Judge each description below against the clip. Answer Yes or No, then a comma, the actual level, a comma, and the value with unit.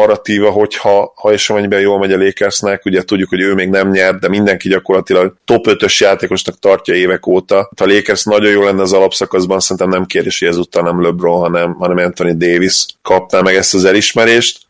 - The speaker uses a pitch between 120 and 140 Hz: No, very low, 95 Hz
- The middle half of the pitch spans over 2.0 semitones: No, narrow, 1.7 semitones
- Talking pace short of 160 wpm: No, fast, 190 wpm